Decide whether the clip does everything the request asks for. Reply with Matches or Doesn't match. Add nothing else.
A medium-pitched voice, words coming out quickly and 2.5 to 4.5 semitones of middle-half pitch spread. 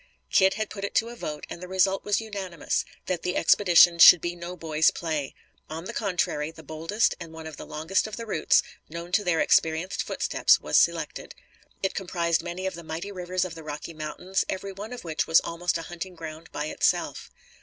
Matches